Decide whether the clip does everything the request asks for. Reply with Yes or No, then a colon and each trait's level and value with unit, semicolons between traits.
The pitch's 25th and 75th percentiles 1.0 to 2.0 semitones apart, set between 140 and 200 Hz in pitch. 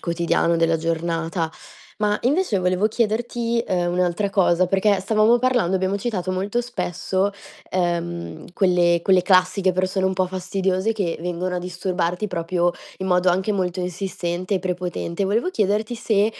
No: narrow, 2.5 semitones; medium, 185 Hz